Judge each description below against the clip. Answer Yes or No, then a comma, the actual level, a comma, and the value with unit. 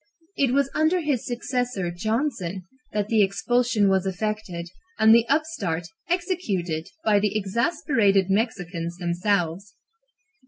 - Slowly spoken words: Yes, slow, 115 wpm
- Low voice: No, high, 210 Hz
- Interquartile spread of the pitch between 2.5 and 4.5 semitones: No, average, 5.0 semitones